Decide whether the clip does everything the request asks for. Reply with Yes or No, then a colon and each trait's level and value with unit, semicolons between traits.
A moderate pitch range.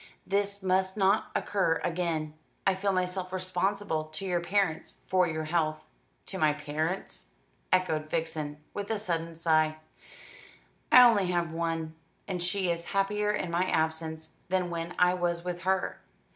Yes: average, 3.0 semitones